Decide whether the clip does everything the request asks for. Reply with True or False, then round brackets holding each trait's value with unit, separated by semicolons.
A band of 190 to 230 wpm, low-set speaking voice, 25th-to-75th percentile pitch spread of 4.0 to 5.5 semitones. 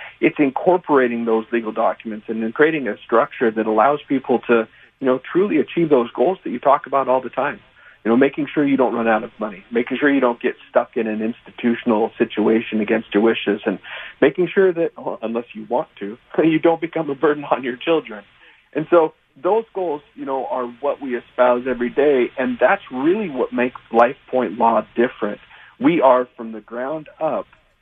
True (205 wpm; 125 Hz; 4.5 semitones)